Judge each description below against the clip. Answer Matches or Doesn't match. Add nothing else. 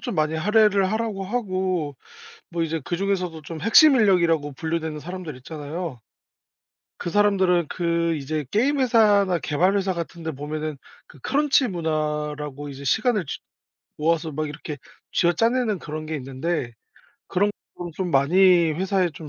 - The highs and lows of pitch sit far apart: Doesn't match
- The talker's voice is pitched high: Doesn't match